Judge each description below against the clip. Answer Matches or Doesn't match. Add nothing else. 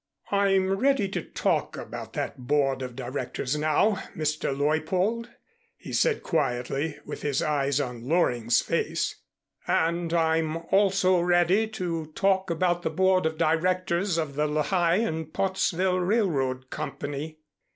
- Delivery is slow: Matches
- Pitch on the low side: Doesn't match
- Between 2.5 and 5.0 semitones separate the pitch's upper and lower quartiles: Matches